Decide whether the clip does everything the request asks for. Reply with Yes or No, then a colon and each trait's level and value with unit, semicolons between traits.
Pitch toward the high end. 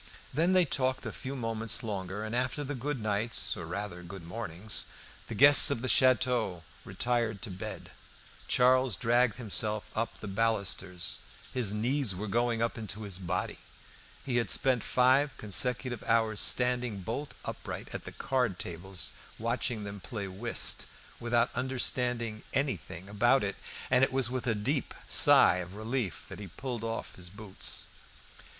No: low, 115 Hz